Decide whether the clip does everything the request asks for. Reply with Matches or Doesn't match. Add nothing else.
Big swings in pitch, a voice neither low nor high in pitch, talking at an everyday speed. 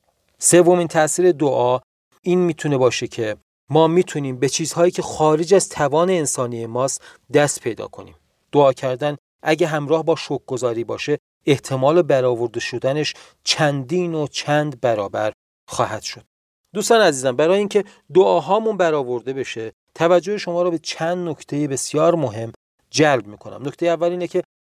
Doesn't match